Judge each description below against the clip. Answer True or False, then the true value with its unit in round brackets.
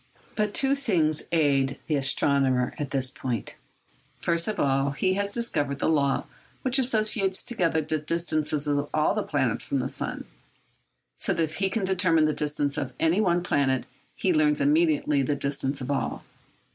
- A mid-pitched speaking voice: True (155 Hz)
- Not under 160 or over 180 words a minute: True (170 wpm)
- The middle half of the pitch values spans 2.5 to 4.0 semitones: False (4.6 semitones)